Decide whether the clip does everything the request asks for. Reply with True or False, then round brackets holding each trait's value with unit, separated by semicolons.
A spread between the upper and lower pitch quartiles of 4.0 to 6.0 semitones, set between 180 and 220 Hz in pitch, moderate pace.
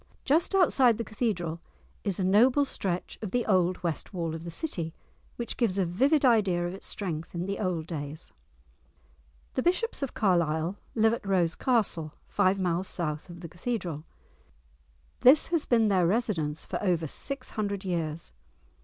True (5.4 semitones; 185 Hz; 165 wpm)